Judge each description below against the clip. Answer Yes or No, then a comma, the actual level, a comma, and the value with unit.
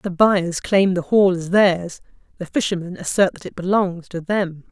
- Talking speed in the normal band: Yes, average, 190 wpm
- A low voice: No, medium, 185 Hz